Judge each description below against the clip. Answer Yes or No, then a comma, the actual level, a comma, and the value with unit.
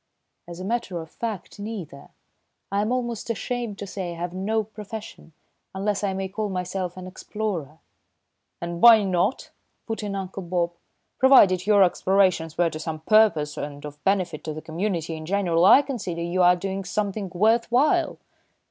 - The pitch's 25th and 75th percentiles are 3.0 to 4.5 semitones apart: Yes, average, 3.7 semitones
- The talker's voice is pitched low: No, high, 190 Hz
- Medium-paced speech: Yes, average, 170 wpm